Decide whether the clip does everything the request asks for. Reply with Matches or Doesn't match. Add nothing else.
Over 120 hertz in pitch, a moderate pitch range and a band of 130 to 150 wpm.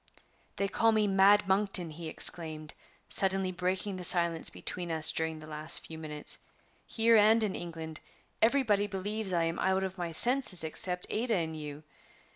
Doesn't match